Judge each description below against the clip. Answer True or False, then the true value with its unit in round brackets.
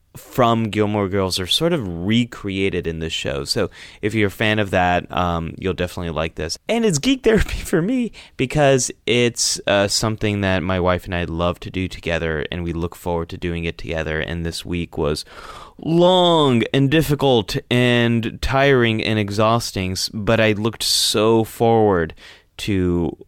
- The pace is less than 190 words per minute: True (170 wpm)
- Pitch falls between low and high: False (105 Hz)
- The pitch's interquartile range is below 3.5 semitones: False (5.3 semitones)